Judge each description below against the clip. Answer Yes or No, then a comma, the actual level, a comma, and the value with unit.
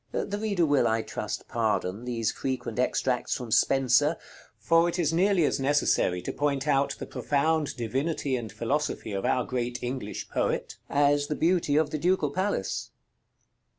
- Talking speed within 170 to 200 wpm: No, average, 160 wpm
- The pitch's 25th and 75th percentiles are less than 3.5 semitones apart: No, average, 4.4 semitones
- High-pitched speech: No, medium, 140 Hz